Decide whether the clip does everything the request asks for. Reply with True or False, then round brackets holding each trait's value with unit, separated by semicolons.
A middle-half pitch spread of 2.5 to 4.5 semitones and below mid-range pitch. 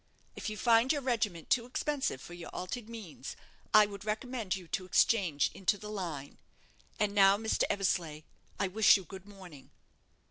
False (3.6 semitones; 200 Hz)